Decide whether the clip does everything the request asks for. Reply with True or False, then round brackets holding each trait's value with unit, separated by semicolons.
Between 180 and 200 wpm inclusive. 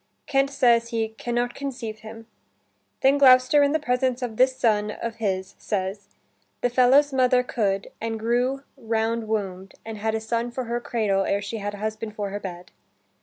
True (185 wpm)